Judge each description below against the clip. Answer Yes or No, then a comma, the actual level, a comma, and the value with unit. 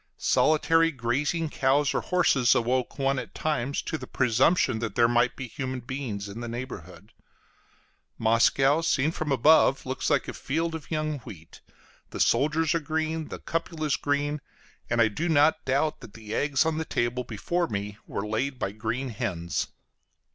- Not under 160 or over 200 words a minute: Yes, average, 170 wpm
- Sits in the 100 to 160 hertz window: Yes, low, 135 Hz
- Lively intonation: No, average, 4.9 semitones